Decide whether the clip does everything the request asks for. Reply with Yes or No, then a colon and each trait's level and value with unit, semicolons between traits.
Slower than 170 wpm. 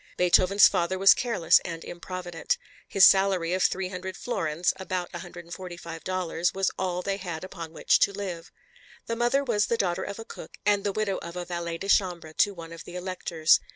No: average, 185 wpm